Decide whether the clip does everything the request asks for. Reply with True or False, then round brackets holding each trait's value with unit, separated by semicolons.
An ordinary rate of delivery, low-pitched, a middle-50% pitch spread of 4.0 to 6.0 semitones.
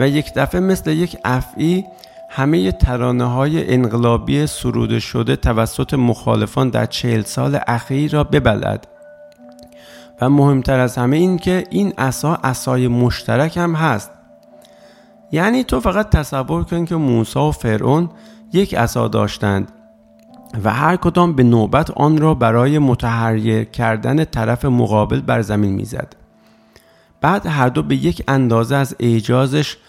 True (135 wpm; 125 Hz; 5.2 semitones)